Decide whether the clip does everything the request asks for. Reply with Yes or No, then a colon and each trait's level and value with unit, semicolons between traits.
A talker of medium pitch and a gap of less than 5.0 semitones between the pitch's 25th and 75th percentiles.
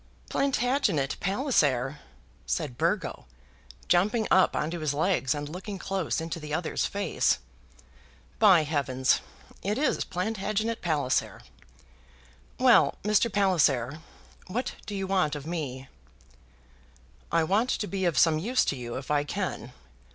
No: medium, 175 Hz; wide, 5.6 semitones